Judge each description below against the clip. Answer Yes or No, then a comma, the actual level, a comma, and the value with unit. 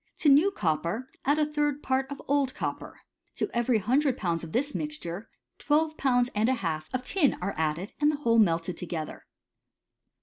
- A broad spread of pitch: Yes, wide, 8.4 semitones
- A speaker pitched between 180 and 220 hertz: No, very high, 250 Hz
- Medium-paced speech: Yes, average, 180 wpm